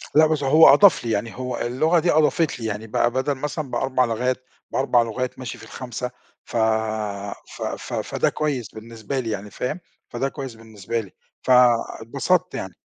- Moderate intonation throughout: Yes, average, 3.5 semitones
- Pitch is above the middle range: No, low, 125 Hz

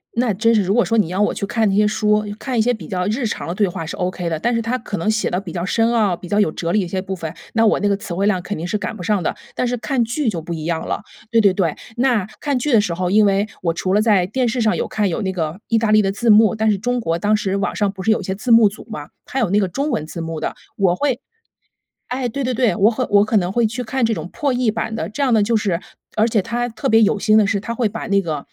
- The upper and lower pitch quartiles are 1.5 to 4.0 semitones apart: Yes, average, 3.6 semitones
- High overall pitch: Yes, high, 210 Hz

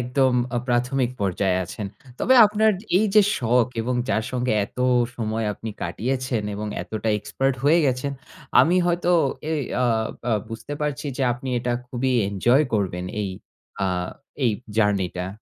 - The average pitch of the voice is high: No, low, 120 Hz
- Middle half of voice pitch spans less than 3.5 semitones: No, average, 4.1 semitones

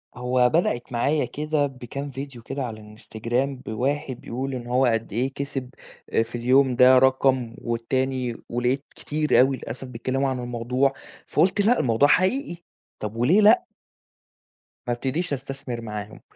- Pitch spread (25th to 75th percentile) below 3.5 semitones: Yes, narrow, 2.5 semitones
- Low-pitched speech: Yes, low, 130 Hz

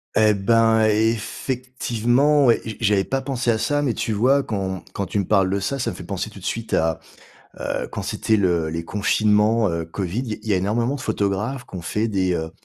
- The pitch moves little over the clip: No, average, 3.4 semitones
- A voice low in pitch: Yes, low, 110 Hz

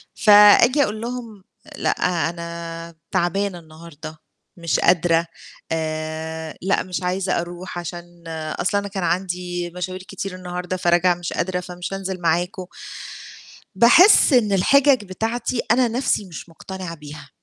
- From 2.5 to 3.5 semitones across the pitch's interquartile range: Yes, average, 2.9 semitones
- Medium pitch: Yes, medium, 180 Hz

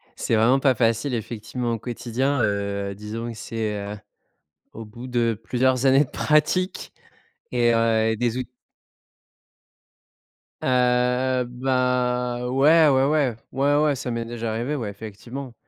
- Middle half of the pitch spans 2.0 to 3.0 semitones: Yes, narrow, 2.5 semitones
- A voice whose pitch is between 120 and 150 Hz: Yes, low, 125 Hz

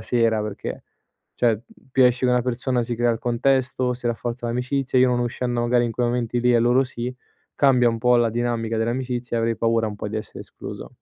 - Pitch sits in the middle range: No, low, 120 Hz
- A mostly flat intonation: Yes, narrow, 1.3 semitones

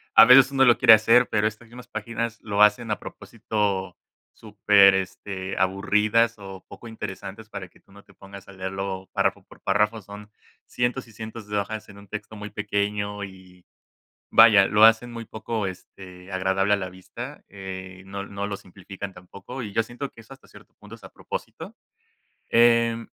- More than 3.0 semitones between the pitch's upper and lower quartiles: No, average, 2.7 semitones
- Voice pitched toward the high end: No, low, 105 Hz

